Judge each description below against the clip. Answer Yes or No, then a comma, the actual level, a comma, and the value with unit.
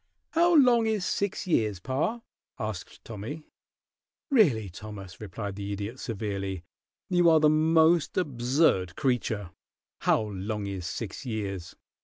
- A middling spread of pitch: No, wide, 8.2 semitones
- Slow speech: Yes, slow, 125 wpm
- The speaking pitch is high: No, low, 115 Hz